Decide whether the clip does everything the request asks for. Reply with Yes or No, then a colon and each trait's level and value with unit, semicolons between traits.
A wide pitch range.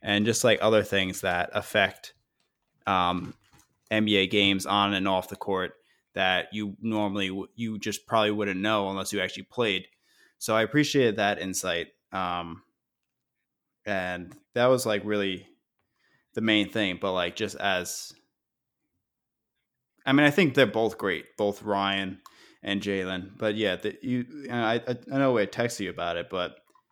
No: narrow, 2.5 semitones